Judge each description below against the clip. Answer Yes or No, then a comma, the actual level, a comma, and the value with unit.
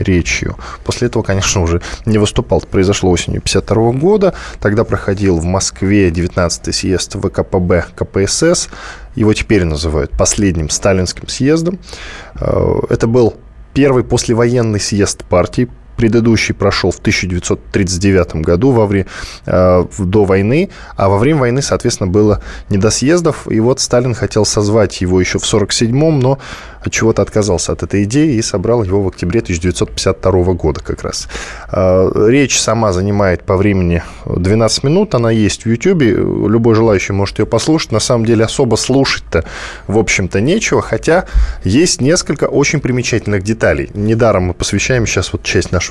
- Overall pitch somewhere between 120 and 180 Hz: No, low, 105 Hz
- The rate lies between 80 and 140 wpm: No, average, 150 wpm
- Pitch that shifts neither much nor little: Yes, average, 4.0 semitones